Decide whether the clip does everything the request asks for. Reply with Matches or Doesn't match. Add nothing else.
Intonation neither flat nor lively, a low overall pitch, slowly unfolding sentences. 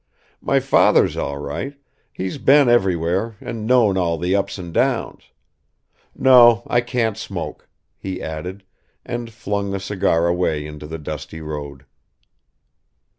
Doesn't match